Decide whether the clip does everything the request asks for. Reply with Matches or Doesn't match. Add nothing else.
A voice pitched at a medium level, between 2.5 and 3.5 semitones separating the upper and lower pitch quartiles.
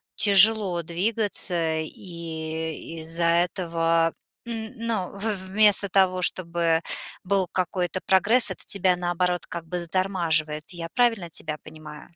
Matches